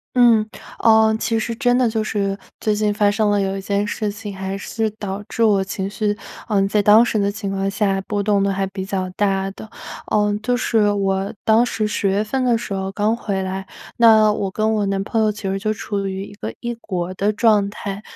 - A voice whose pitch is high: Yes, high, 205 Hz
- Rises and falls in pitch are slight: Yes, narrow, 2.0 semitones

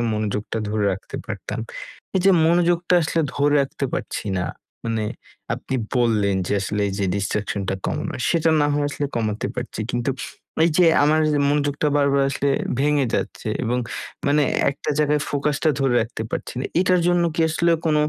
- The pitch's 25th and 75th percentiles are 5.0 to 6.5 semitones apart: Yes, wide, 5.4 semitones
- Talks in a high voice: No, medium, 140 Hz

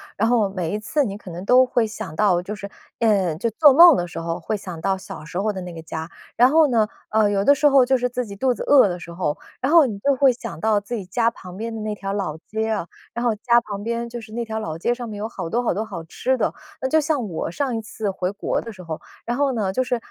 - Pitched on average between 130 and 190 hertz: No, high, 215 Hz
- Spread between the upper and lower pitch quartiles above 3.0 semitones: Yes, average, 4.4 semitones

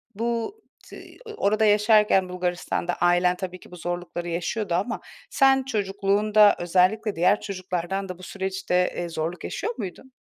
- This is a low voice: No, high, 190 Hz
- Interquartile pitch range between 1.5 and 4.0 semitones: Yes, average, 3.1 semitones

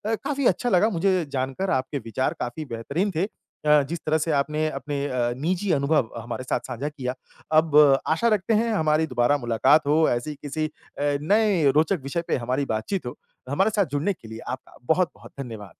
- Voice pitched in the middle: Yes, medium, 150 Hz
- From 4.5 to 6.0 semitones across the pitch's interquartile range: Yes, average, 4.8 semitones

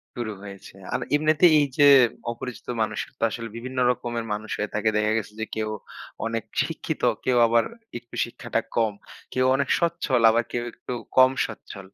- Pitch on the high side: No, low, 115 Hz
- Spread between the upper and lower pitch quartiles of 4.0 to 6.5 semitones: No, average, 2.7 semitones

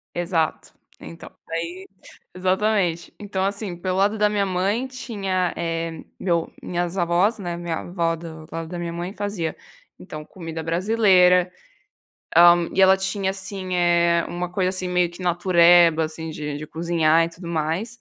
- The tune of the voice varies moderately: No, narrow, 2.3 semitones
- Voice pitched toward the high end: No, medium, 175 Hz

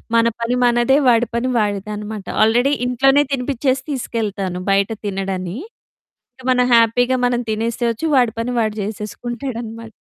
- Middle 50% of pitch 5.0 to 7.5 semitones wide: No, average, 2.8 semitones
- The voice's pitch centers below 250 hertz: Yes, high, 230 Hz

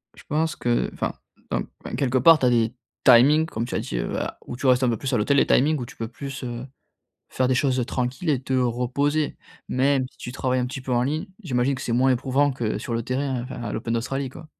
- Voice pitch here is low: Yes, low, 130 Hz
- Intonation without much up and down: Yes, narrow, 2.3 semitones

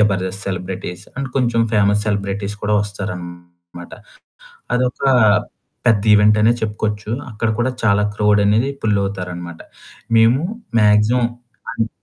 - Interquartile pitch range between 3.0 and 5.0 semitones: No, narrow, 2.5 semitones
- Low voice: Yes, low, 105 Hz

